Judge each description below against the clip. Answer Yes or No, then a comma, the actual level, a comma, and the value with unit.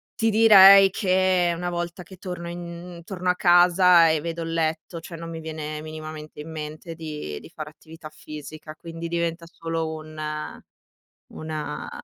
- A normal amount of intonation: No, narrow, 2.1 semitones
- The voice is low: No, medium, 165 Hz